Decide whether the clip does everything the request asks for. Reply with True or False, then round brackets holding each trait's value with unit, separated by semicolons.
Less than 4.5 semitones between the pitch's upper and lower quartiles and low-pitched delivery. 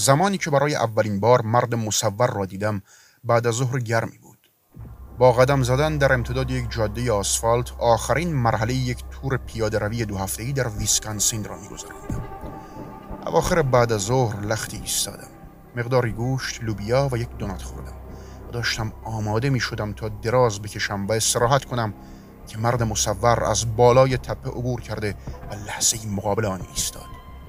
True (3.1 semitones; 115 Hz)